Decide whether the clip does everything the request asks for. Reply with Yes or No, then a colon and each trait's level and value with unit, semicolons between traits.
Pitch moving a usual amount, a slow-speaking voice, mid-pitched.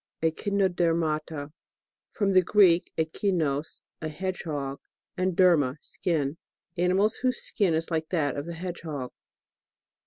Yes: average, 3.3 semitones; slow, 130 wpm; medium, 165 Hz